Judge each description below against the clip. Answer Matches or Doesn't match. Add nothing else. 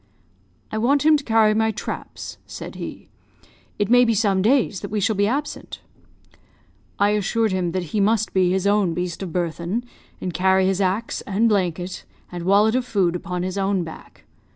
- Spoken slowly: Doesn't match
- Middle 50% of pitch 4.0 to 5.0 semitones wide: Doesn't match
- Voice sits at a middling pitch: Doesn't match